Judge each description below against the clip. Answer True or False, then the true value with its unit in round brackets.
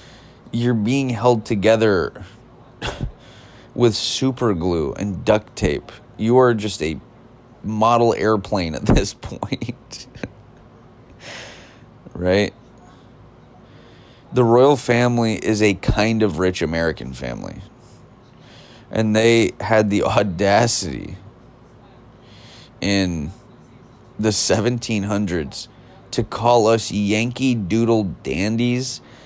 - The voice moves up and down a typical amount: True (3.1 semitones)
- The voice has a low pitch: True (110 Hz)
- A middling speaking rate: False (90 wpm)